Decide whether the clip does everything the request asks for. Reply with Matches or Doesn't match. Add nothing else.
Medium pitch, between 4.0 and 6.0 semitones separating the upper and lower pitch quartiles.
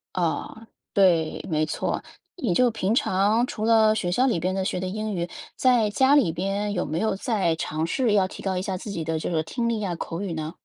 Doesn't match